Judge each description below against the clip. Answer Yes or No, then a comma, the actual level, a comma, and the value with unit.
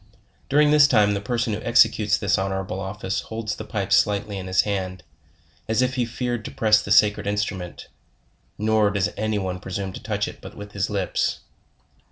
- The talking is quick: No, average, 190 wpm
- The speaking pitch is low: Yes, low, 105 Hz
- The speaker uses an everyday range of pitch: No, narrow, 2.3 semitones